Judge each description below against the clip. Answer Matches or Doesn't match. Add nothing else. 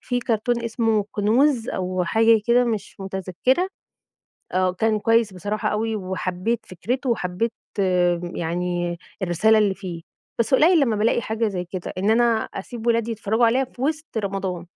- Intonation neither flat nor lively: Matches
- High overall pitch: Matches